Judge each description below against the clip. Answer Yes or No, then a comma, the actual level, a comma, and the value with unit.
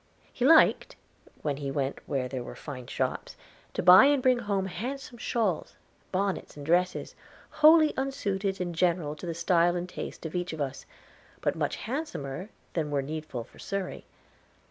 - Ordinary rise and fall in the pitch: No, wide, 6.6 semitones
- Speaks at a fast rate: No, average, 165 wpm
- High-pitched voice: No, medium, 180 Hz